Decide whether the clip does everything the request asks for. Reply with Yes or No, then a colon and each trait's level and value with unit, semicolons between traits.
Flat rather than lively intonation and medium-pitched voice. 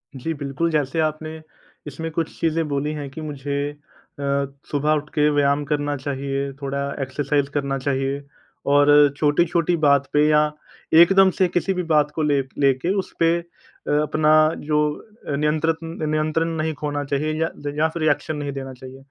Yes: narrow, 2.0 semitones; medium, 150 Hz